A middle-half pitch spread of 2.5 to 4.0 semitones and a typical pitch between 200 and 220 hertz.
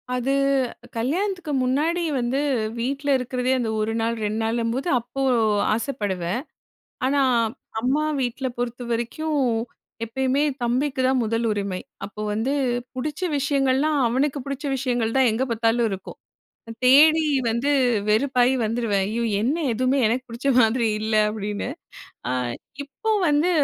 No: average, 3.4 semitones; very high, 250 Hz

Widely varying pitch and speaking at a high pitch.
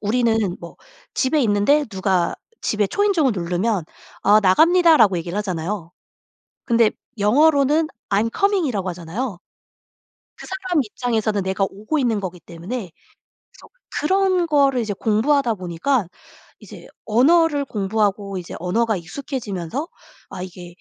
Yes: wide, 7.0 semitones; high, 215 Hz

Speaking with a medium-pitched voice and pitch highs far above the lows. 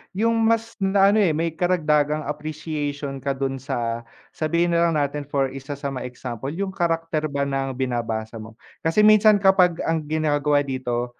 No: medium, 150 Hz; average, 4.1 semitones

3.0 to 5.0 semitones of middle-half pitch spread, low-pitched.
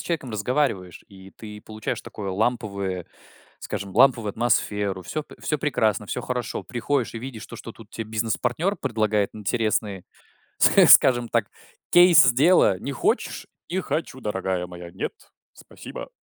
Yes: average, 4.2 semitones; low, 110 Hz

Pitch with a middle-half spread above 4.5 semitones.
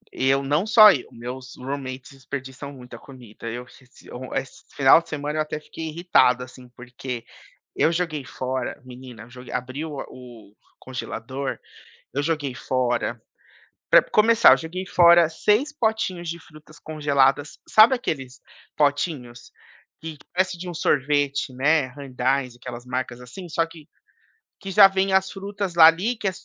Yes: average, 4.9 semitones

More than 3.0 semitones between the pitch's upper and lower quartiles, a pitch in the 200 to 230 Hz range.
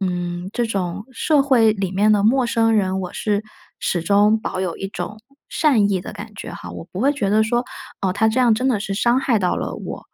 Yes: average, 3.6 semitones; high, 210 Hz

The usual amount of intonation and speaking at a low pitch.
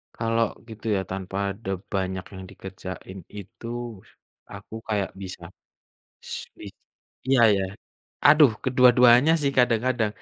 Yes: average, 4.3 semitones; low, 110 Hz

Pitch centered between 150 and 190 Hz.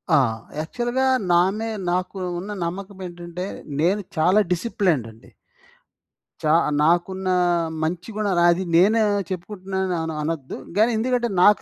Yes: medium, 185 Hz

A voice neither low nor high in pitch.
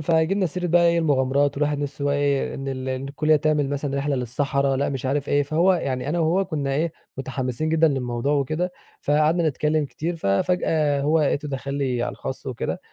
Yes: medium, 145 Hz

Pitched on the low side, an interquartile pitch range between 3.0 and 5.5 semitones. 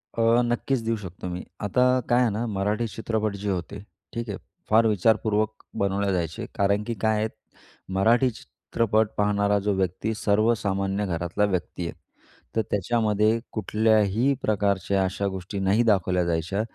No: low, 105 Hz; narrow, 2.4 semitones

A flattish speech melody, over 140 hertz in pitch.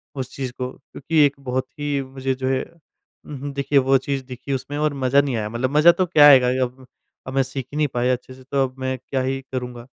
No: narrow, 1.6 semitones; low, 135 Hz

